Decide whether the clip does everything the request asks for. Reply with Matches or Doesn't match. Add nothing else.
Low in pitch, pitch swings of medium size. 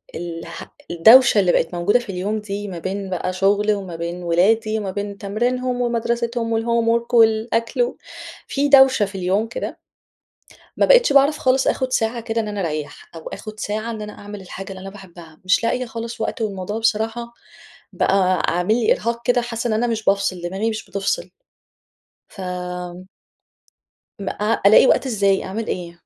Doesn't match